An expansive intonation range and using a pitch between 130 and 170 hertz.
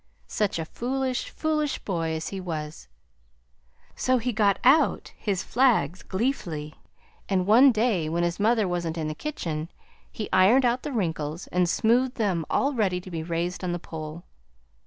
No: wide, 6.4 semitones; high, 190 Hz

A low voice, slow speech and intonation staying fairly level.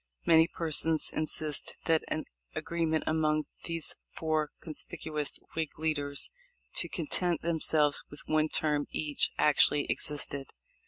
No: medium, 155 Hz; slow, 125 wpm; narrow, 1.4 semitones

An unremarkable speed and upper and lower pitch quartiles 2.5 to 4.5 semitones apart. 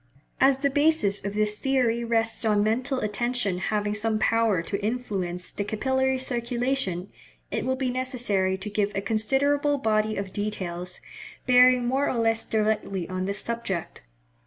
Yes: average, 155 wpm; average, 3.9 semitones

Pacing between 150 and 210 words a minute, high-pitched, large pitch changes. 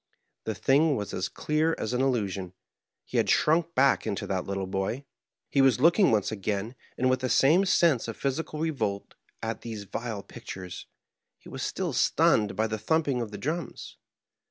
No: average, 180 wpm; low, 120 Hz; wide, 6.1 semitones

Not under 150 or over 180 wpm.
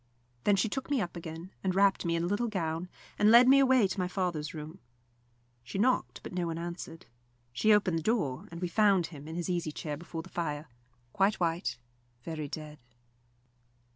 No: average, 200 wpm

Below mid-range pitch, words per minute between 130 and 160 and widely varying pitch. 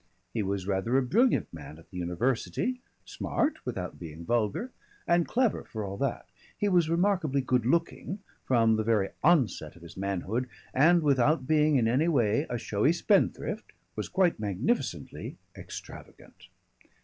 Yes: low, 125 Hz; average, 150 wpm; wide, 8.8 semitones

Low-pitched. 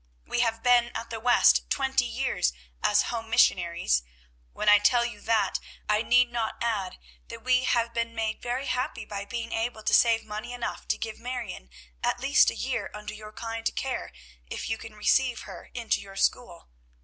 No: high, 230 Hz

